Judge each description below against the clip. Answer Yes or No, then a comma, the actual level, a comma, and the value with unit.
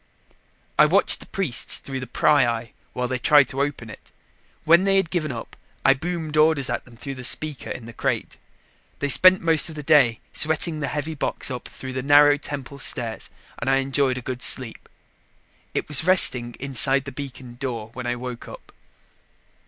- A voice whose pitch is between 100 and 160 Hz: Yes, low, 135 Hz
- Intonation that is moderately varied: Yes, average, 3.4 semitones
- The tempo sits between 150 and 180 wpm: No, average, 190 wpm